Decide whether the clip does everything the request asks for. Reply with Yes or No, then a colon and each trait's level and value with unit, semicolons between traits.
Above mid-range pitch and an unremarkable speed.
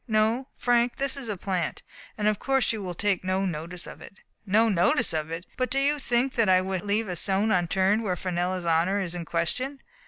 No: high, 195 Hz; fast, 220 wpm